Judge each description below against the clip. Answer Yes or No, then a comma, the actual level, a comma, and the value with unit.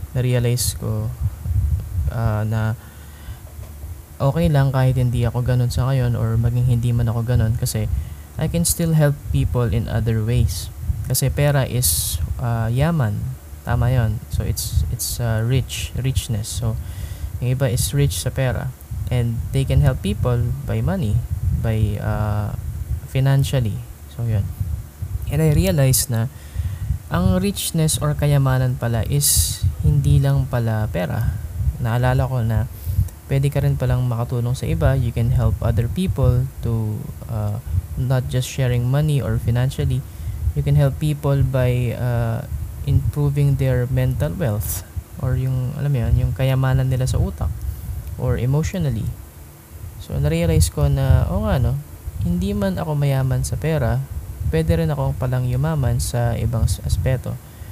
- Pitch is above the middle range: No, low, 115 Hz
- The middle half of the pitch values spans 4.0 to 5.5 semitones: Yes, average, 4.9 semitones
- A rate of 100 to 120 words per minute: No, average, 145 wpm